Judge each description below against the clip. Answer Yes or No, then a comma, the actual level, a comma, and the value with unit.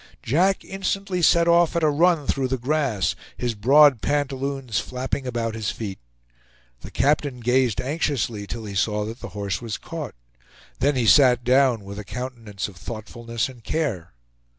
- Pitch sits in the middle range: No, low, 125 Hz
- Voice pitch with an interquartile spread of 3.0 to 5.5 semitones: Yes, average, 4.7 semitones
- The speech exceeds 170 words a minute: No, average, 165 wpm